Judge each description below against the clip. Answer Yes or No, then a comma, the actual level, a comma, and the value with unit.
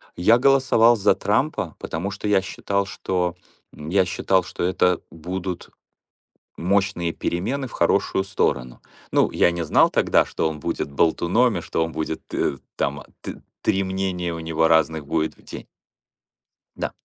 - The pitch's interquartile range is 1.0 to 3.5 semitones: Yes, average, 3.2 semitones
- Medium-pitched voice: No, very low, 90 Hz